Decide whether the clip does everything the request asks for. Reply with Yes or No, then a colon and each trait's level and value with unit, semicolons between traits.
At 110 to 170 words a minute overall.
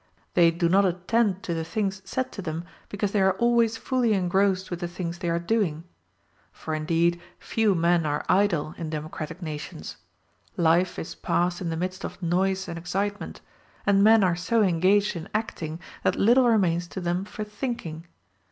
No: average, 180 wpm